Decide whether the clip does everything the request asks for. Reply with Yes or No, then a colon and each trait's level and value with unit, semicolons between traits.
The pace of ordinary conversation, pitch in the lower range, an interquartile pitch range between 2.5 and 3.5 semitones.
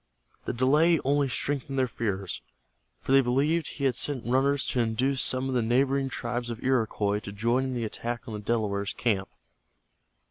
Yes: average, 180 wpm; low, 125 Hz; average, 3.2 semitones